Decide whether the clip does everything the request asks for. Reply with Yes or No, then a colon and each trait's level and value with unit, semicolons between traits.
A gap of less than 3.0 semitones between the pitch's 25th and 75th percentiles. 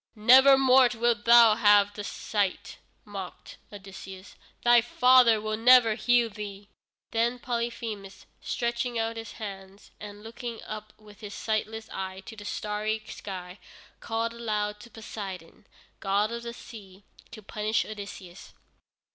Yes: narrow, 2.5 semitones